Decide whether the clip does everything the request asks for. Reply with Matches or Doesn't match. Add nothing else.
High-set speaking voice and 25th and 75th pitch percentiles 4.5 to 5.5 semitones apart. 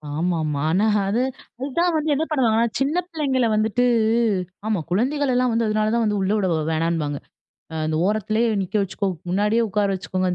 Matches